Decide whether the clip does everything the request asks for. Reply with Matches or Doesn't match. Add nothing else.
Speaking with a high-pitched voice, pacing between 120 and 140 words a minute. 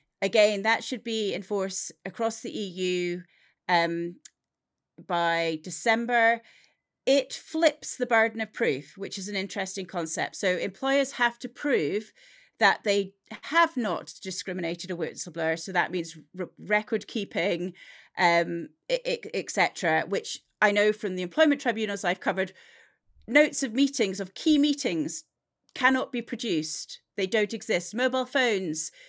Matches